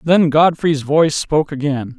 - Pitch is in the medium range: Yes, medium, 150 Hz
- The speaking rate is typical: Yes, average, 150 wpm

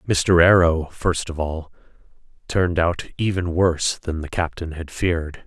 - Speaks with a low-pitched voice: Yes, very low, 85 Hz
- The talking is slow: No, average, 155 wpm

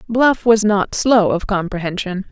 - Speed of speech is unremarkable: Yes, average, 155 wpm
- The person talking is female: Yes, female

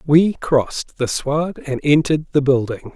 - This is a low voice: No, medium, 150 Hz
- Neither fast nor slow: Yes, average, 165 wpm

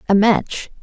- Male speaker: No, female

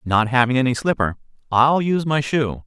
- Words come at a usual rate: Yes, average, 180 wpm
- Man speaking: Yes, male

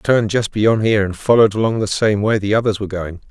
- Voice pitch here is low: Yes, low, 105 Hz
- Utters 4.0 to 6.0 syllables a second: No, 6.5 syllables/s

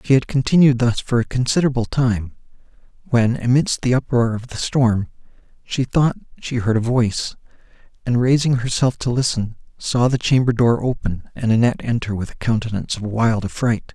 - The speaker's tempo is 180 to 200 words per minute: No, average, 170 wpm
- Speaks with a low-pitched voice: Yes, low, 120 Hz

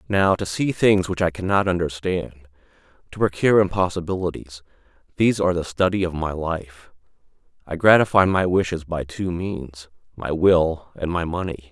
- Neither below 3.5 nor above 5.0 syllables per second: No, 5.2 syllables/s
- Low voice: Yes, very low, 85 Hz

